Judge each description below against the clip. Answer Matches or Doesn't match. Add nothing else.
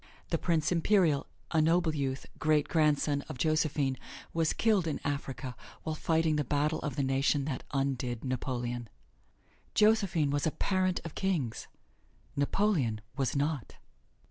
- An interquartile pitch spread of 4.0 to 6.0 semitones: Doesn't match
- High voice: Doesn't match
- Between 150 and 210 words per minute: Doesn't match